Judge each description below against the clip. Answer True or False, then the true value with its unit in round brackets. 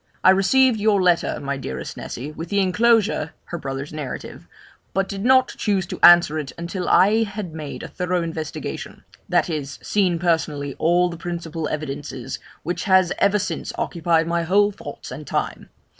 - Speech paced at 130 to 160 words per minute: False (170 wpm)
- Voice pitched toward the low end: False (175 Hz)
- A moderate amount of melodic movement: True (4.1 semitones)